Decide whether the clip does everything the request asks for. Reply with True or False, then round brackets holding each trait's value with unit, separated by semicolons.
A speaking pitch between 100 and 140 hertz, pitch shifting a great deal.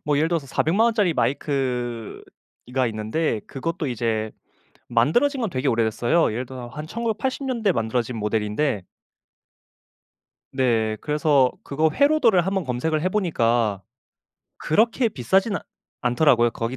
True (135 Hz; 7.3 semitones)